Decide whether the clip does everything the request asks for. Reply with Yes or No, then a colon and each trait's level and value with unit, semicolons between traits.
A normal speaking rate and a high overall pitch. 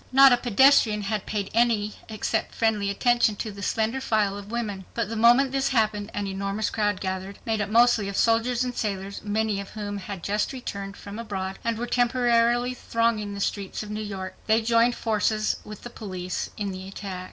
Yes: average, 195 wpm; high, 215 Hz